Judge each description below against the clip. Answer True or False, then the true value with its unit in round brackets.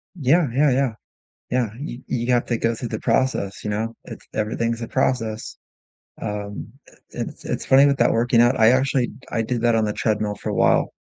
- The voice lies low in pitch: True (120 Hz)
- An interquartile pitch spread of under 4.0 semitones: True (2.8 semitones)